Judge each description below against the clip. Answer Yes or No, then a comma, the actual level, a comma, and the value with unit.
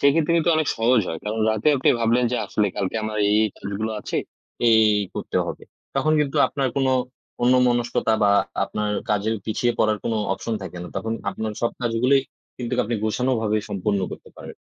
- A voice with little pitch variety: No, average, 3.0 semitones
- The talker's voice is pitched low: Yes, low, 115 Hz